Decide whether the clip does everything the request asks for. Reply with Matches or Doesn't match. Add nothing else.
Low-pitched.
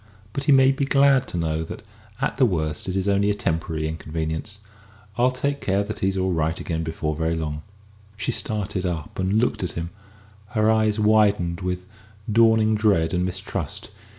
Matches